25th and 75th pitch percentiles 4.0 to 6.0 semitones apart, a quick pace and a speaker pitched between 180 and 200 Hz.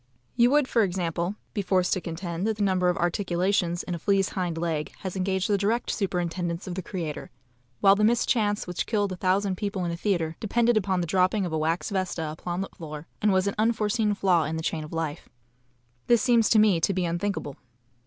No: average, 3.2 semitones; fast, 215 wpm; medium, 185 Hz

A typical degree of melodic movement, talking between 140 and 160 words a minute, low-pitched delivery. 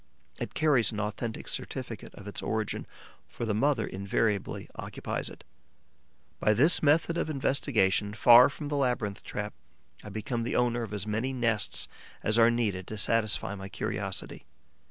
Yes: average, 3.2 semitones; average, 155 wpm; low, 110 Hz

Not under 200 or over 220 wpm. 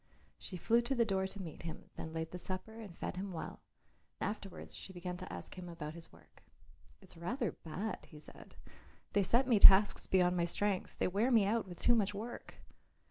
Yes: fast, 205 wpm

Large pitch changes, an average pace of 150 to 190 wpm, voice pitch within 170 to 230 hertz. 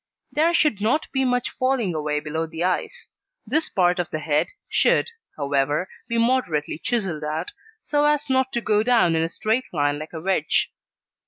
Yes: wide, 8.6 semitones; average, 180 wpm; high, 190 Hz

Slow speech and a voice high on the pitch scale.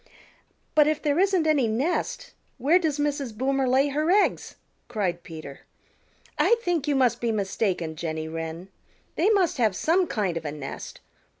No: average, 165 wpm; very high, 260 Hz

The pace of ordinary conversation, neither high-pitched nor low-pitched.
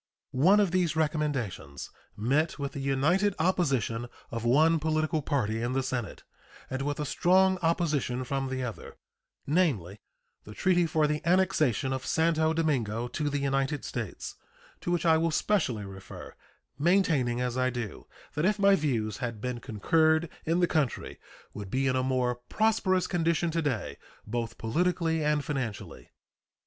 Yes: average, 160 wpm; medium, 145 Hz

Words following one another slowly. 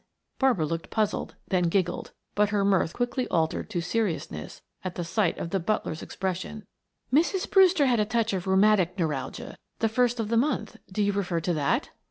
No: average, 180 wpm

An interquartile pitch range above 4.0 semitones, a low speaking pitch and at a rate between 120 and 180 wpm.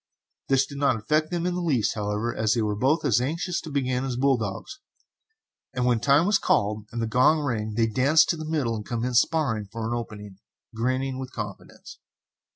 No: average, 4.7 semitones; low, 125 Hz; fast, 205 wpm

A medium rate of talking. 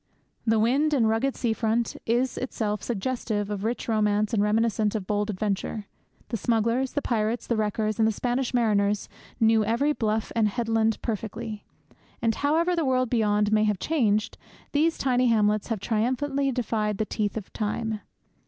Yes: average, 165 wpm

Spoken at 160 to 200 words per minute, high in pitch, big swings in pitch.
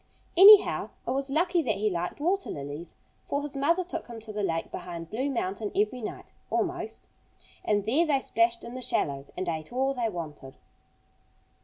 Yes: average, 180 wpm; high, 230 Hz; wide, 7.9 semitones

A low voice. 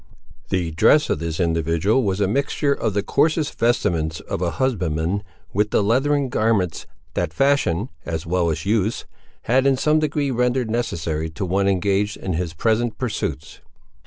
Yes: low, 100 Hz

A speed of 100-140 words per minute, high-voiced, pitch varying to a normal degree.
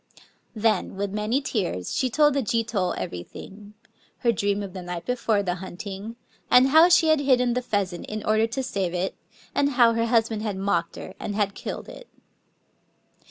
No: average, 185 wpm; high, 215 Hz; average, 4.3 semitones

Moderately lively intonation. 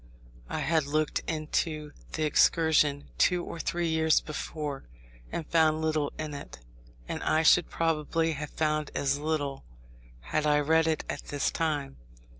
No: narrow, 1.5 semitones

